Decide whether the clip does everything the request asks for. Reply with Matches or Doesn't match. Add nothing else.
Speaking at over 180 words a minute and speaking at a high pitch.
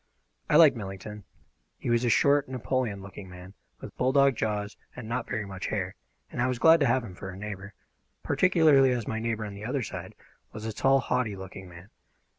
Doesn't match